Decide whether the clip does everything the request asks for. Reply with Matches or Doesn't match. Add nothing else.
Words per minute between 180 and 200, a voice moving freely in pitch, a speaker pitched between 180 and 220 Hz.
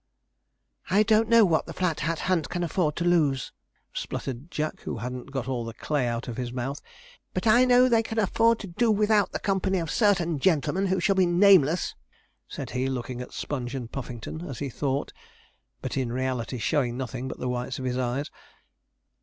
Doesn't match